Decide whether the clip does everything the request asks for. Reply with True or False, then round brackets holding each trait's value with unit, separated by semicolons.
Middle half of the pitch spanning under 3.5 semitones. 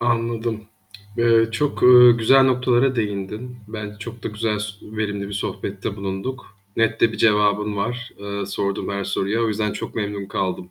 True (2.6 semitones)